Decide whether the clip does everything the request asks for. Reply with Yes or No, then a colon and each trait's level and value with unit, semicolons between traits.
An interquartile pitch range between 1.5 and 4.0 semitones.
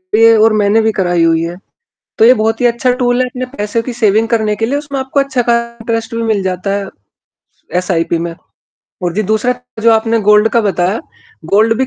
Yes: average, 2.7 semitones